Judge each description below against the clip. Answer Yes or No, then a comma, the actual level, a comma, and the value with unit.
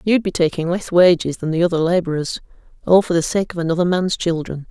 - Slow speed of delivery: No, fast, 205 wpm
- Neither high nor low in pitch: Yes, medium, 175 Hz